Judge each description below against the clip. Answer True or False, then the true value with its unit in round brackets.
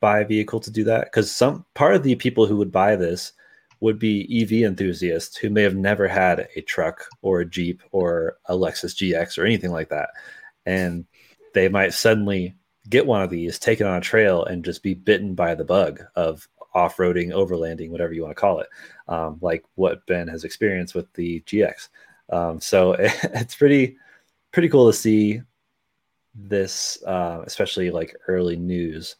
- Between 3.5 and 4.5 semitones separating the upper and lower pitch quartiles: True (3.9 semitones)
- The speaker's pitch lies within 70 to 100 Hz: True (95 Hz)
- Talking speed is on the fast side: False (185 wpm)